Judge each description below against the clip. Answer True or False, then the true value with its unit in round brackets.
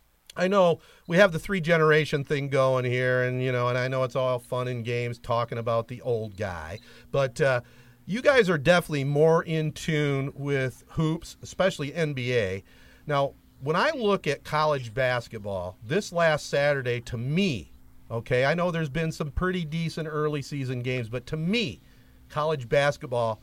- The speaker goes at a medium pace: True (170 wpm)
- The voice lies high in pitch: False (140 Hz)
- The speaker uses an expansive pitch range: False (4.7 semitones)